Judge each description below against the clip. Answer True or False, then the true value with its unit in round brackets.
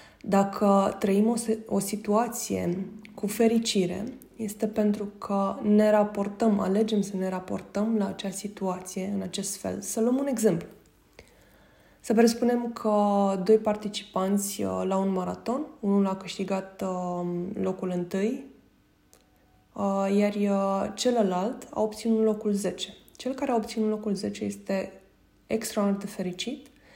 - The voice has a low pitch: False (205 Hz)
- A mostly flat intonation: True (2.2 semitones)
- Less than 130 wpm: True (120 wpm)